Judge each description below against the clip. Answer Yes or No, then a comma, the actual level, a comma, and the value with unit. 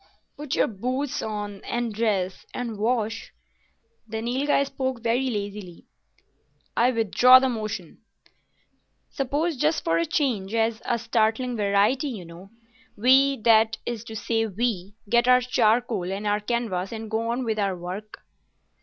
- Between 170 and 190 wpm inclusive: No, slow, 135 wpm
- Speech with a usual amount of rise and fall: Yes, average, 3.2 semitones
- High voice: Yes, high, 225 Hz